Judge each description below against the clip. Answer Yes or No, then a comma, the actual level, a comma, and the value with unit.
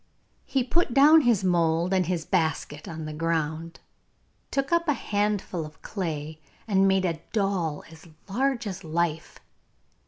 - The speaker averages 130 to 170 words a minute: Yes, average, 150 wpm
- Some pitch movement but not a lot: Yes, average, 4.7 semitones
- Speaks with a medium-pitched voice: Yes, medium, 180 Hz